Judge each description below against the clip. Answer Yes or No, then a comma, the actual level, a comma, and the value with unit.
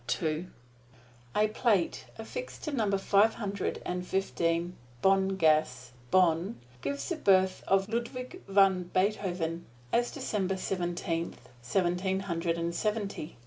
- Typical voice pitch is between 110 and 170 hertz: No, high, 190 Hz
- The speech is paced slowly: Yes, slow, 100 wpm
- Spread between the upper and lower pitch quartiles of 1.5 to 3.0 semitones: No, average, 3.4 semitones